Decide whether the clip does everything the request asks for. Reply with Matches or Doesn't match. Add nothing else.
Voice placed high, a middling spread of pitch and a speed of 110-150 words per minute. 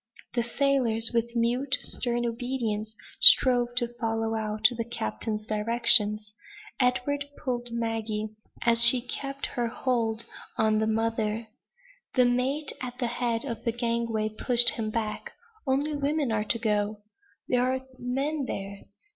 Doesn't match